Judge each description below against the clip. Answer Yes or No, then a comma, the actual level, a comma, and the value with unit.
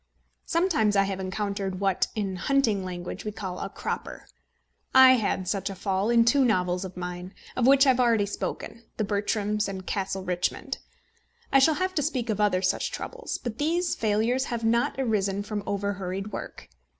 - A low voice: No, high, 205 Hz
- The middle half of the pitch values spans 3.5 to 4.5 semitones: Yes, average, 3.9 semitones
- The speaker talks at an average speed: Yes, average, 185 wpm